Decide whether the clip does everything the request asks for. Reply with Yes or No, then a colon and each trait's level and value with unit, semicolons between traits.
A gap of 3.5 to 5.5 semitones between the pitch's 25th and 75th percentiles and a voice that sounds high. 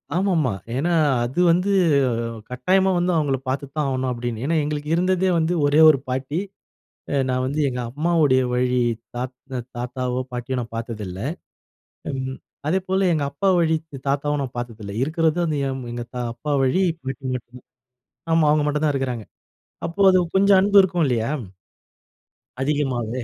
No: average, 4.6 semitones; medium, 140 Hz